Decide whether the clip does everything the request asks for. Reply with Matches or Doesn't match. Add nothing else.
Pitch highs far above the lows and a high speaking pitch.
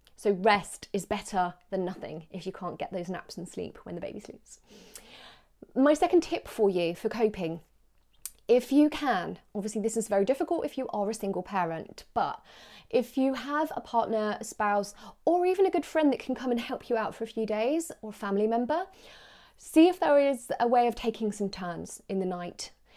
Matches